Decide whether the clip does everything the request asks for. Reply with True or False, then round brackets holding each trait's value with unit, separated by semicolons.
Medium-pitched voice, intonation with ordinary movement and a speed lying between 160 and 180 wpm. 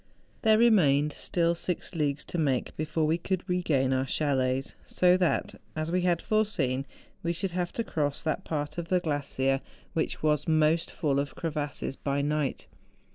True (155 Hz; 3.6 semitones; 170 wpm)